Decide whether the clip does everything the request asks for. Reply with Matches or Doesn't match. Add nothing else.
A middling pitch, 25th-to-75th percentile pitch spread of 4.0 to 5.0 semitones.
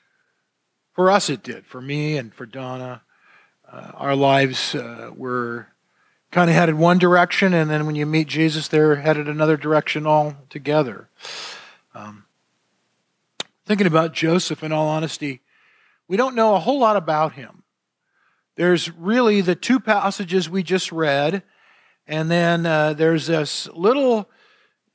Matches